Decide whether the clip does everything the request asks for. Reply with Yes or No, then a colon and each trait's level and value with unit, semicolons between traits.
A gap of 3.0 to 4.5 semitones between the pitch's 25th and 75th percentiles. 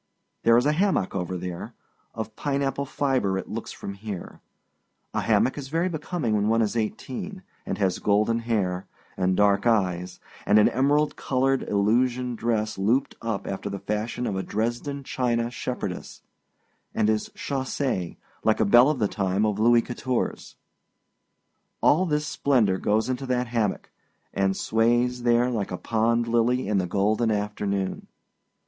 Yes: average, 4.0 semitones